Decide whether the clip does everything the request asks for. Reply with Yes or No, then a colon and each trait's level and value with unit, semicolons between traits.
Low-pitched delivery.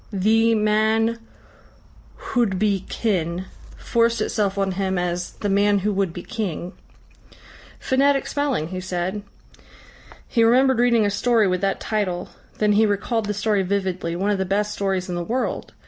No: high, 205 Hz